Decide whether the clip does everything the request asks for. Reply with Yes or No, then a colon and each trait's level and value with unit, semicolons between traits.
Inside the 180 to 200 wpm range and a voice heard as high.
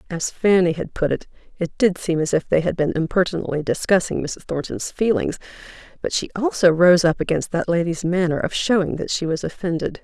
No: average, 195 wpm; medium, 170 Hz